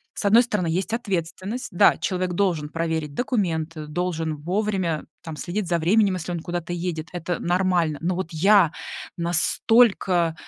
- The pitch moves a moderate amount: Yes, average, 3.0 semitones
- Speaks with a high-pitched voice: No, medium, 175 Hz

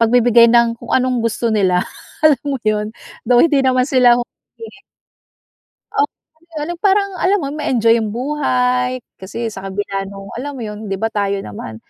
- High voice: Yes, high, 235 Hz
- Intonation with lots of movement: No, average, 3.6 semitones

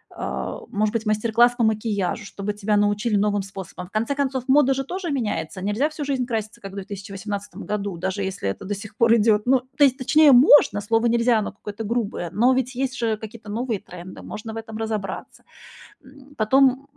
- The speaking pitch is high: Yes, high, 220 Hz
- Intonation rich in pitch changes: No, average, 3.6 semitones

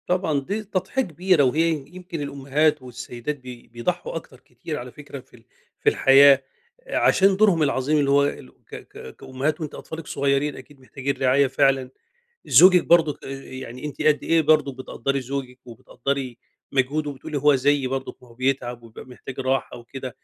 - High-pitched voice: No, medium, 140 Hz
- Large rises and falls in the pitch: No, average, 2.9 semitones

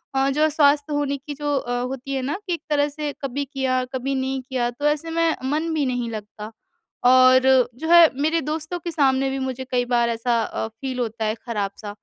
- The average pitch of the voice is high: Yes, very high, 270 Hz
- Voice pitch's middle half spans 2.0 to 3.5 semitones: Yes, average, 3.1 semitones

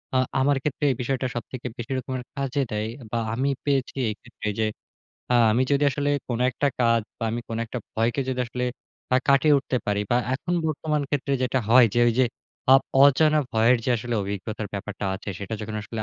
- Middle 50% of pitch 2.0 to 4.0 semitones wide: Yes, average, 3.3 semitones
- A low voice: Yes, low, 125 Hz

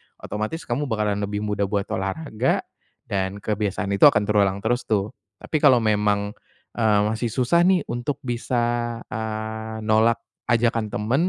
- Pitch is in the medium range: No, low, 110 Hz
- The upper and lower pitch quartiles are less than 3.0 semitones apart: Yes, narrow, 2.5 semitones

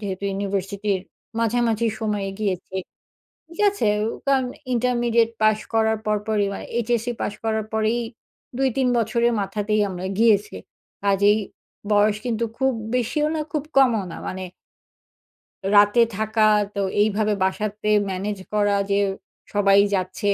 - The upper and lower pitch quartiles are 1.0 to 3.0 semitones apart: Yes, narrow, 2.5 semitones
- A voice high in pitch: Yes, high, 215 Hz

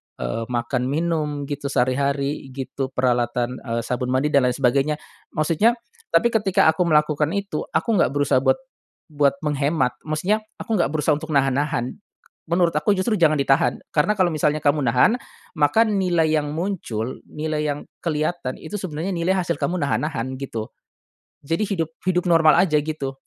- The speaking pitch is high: No, medium, 150 Hz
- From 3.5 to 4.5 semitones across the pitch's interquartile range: Yes, average, 3.8 semitones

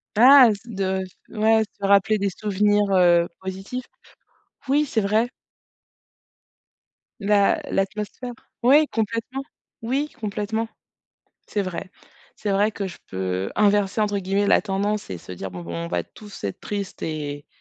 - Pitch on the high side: Yes, high, 205 Hz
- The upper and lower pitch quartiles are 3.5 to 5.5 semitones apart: No, narrow, 2.6 semitones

